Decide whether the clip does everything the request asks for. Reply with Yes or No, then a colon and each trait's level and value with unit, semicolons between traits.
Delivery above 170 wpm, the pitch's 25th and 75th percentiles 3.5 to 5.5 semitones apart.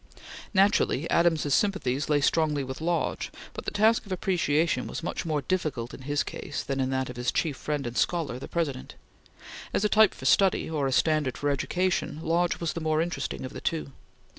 Yes: average, 200 wpm; average, 4.1 semitones